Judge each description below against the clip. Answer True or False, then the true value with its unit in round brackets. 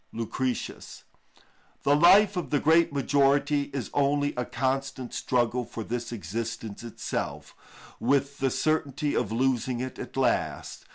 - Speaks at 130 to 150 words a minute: True (140 wpm)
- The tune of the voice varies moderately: True (3.1 semitones)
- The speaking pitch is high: False (135 Hz)